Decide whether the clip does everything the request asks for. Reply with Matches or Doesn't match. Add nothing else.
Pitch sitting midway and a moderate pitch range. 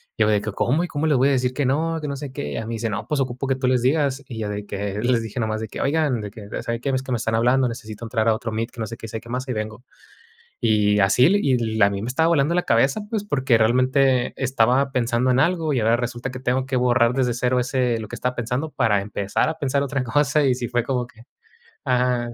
Doesn't match